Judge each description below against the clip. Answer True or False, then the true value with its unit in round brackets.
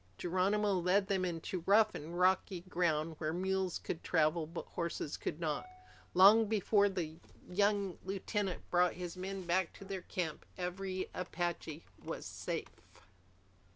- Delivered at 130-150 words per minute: True (140 wpm)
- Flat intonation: True (2.2 semitones)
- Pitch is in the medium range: True (180 Hz)